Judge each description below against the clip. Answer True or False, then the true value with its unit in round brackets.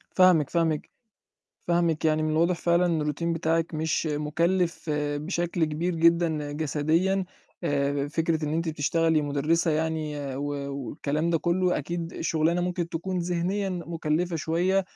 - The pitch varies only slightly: True (2.3 semitones)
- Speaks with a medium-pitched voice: True (165 Hz)